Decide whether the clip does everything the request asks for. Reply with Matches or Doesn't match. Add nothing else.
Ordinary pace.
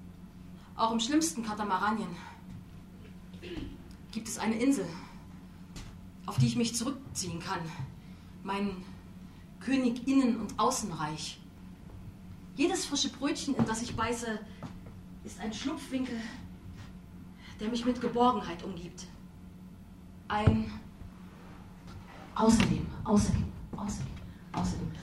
Doesn't match